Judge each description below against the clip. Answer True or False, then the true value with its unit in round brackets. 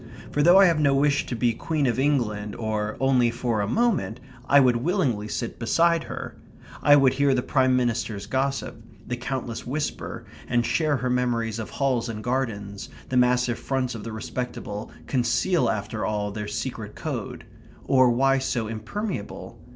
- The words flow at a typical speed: True (170 wpm)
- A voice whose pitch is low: True (125 Hz)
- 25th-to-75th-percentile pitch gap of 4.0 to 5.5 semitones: False (3.5 semitones)